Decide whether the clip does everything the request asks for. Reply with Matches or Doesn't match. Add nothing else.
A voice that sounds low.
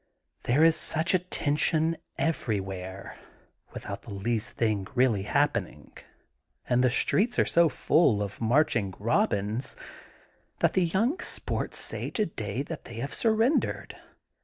Matches